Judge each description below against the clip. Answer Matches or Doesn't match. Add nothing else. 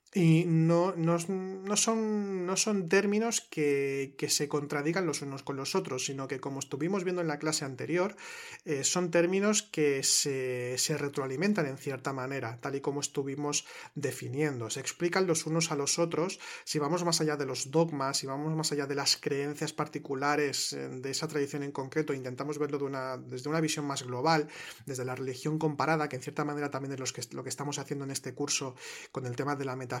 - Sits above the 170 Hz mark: Doesn't match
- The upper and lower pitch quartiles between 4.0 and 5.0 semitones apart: Doesn't match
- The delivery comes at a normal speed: Doesn't match